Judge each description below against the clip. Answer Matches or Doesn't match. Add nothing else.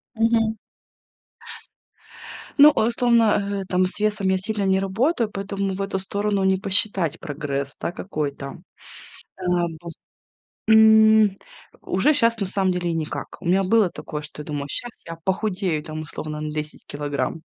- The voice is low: Doesn't match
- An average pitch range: Matches